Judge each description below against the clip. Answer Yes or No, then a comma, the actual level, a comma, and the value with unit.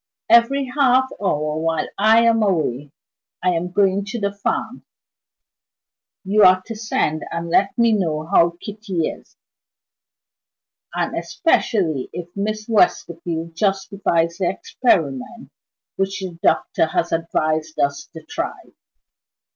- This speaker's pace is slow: Yes, slow, 125 wpm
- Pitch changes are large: No, average, 4.5 semitones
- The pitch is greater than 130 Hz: Yes, medium, 185 Hz